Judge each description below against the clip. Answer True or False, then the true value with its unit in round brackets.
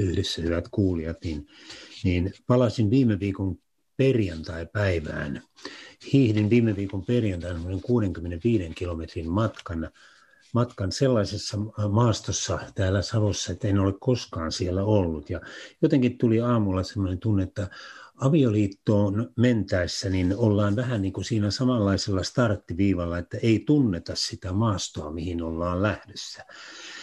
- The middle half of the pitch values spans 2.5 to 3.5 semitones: False (3.9 semitones)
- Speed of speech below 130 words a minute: True (115 wpm)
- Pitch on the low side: True (100 Hz)